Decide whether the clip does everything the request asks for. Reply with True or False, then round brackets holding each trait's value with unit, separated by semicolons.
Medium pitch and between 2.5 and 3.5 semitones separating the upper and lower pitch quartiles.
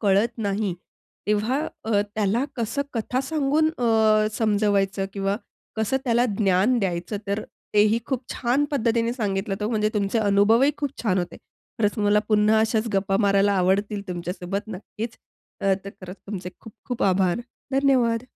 False (210 Hz; 2.8 semitones)